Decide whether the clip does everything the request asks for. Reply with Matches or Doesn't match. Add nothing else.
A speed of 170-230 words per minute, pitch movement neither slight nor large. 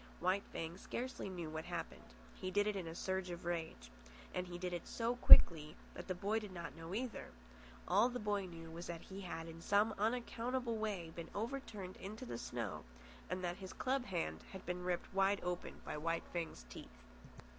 Matches